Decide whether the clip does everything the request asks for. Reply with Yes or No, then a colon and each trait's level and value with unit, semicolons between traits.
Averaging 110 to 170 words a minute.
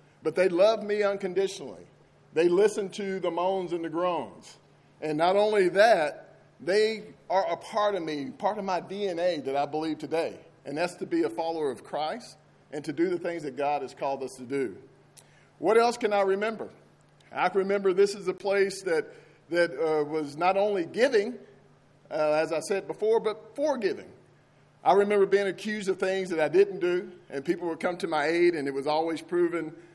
No: average, 195 wpm